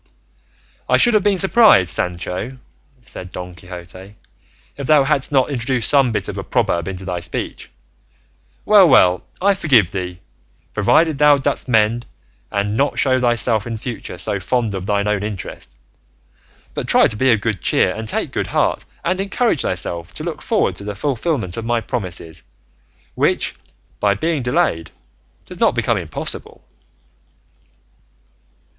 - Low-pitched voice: Yes, low, 110 Hz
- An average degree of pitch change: No, wide, 6.9 semitones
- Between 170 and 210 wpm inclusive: No, average, 150 wpm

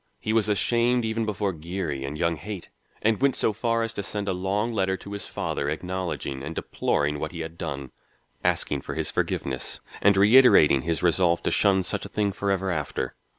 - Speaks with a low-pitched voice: Yes, very low, 95 Hz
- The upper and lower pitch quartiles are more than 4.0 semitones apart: Yes, average, 4.4 semitones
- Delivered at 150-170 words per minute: No, average, 195 wpm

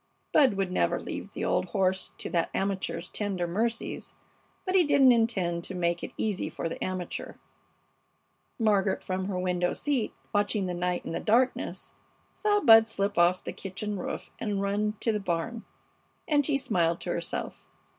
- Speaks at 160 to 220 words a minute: Yes, average, 170 wpm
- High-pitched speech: Yes, high, 200 Hz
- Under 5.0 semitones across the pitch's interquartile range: Yes, average, 3.9 semitones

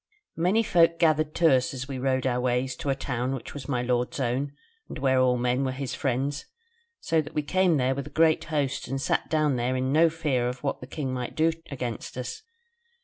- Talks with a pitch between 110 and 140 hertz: Yes, low, 135 Hz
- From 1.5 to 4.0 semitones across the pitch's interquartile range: Yes, average, 3.3 semitones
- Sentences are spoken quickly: Yes, fast, 225 wpm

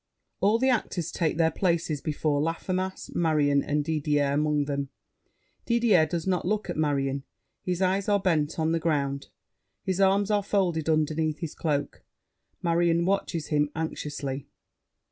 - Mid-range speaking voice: Yes, medium, 160 Hz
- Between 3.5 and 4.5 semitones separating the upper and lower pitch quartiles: Yes, average, 3.9 semitones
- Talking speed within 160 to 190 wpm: No, average, 145 wpm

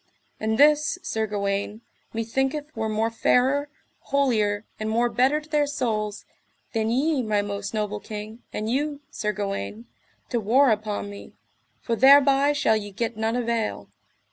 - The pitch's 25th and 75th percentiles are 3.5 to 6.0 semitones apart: Yes, average, 4.3 semitones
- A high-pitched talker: Yes, high, 225 Hz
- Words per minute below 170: Yes, average, 150 wpm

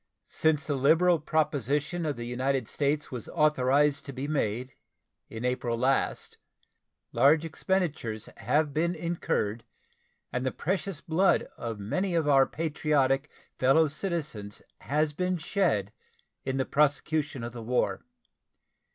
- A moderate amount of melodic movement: Yes, average, 3.8 semitones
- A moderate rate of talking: No, slow, 130 wpm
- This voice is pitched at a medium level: Yes, medium, 145 Hz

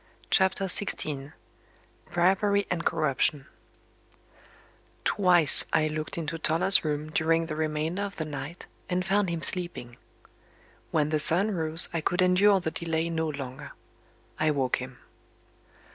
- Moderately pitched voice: Yes, medium, 160 Hz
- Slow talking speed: Yes, slow, 130 wpm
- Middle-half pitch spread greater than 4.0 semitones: No, average, 3.1 semitones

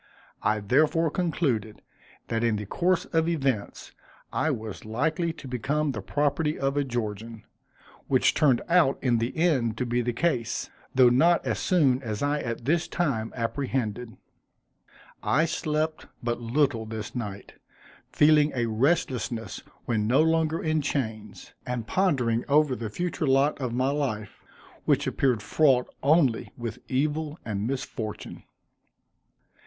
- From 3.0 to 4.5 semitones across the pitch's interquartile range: No, average, 5.0 semitones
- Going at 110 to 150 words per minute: Yes, average, 140 wpm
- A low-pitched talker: Yes, low, 130 Hz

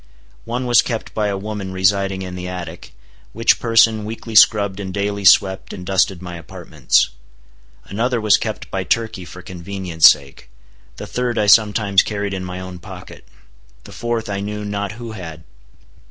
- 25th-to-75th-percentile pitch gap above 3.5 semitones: No, average, 2.9 semitones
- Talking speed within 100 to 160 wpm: No, average, 170 wpm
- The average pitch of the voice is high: No, low, 100 Hz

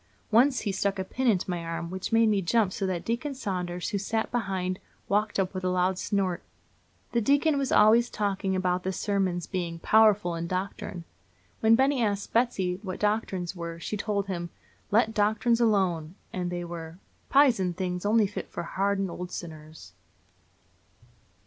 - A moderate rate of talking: Yes, average, 175 wpm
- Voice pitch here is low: No, high, 195 Hz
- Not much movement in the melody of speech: No, average, 3.4 semitones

